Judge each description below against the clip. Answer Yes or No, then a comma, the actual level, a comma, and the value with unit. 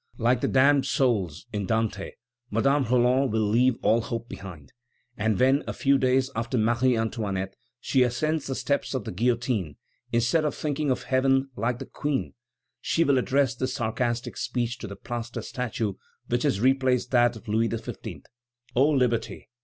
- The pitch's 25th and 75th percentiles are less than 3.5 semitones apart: Yes, average, 2.8 semitones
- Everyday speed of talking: Yes, average, 170 wpm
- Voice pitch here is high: No, low, 120 Hz